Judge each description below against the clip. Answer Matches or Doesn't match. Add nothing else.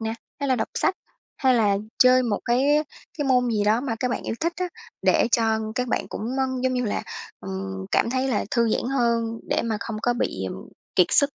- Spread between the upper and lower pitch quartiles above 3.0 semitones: Doesn't match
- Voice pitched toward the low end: Doesn't match